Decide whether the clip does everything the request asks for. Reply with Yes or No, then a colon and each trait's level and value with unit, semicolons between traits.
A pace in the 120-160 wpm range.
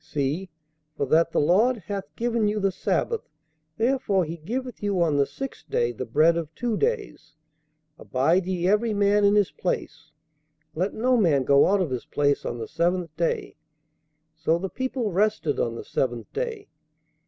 No: average, 175 wpm